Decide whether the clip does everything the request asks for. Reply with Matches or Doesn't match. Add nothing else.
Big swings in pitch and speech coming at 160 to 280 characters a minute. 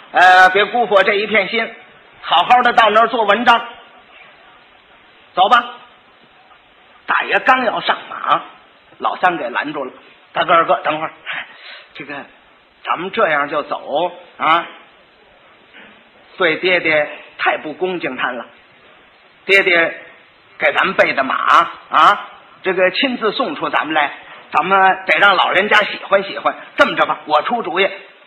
Doesn't match